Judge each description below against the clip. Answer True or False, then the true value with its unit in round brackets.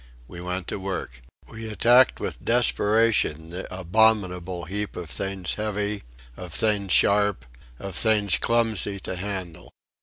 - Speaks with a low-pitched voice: True (100 Hz)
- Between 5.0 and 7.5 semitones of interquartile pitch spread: False (3.1 semitones)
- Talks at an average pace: False (130 wpm)